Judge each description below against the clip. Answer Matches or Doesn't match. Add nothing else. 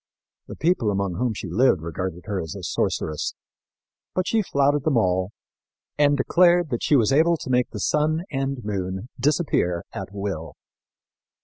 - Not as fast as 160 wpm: Doesn't match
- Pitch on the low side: Matches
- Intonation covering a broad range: Matches